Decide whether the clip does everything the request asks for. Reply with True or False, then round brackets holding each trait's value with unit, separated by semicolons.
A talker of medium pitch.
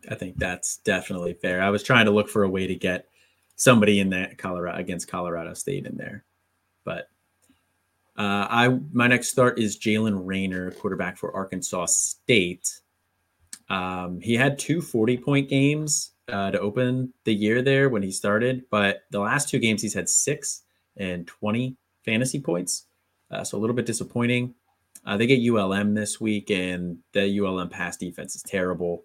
False (105 Hz)